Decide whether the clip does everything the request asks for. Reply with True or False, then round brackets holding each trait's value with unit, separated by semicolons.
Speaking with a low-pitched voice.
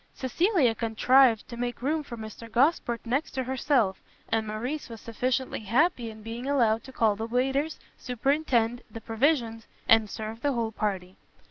False (235 Hz)